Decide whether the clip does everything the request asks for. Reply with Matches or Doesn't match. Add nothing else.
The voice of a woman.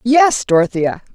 Matches